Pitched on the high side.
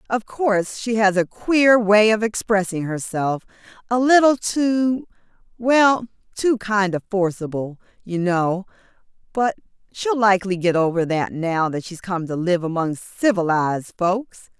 Yes: high, 200 Hz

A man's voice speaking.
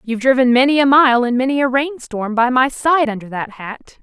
No: female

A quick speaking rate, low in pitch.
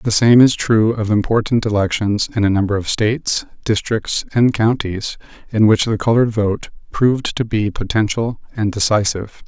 No: average, 165 wpm; low, 110 Hz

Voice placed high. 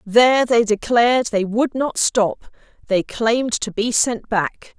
Yes: high, 230 Hz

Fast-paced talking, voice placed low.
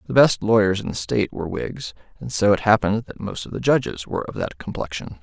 Yes: fast, 240 wpm; low, 100 Hz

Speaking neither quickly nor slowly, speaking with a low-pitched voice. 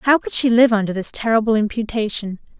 No: average, 185 wpm; high, 225 Hz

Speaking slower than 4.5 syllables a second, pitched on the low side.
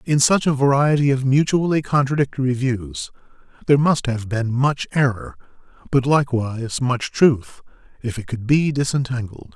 No: 5.0 syllables/s; low, 130 Hz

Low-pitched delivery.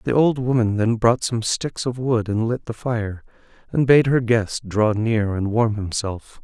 Yes: low, 115 Hz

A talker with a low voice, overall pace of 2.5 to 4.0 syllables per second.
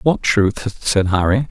Yes: low, 110 Hz; 3.6 syllables/s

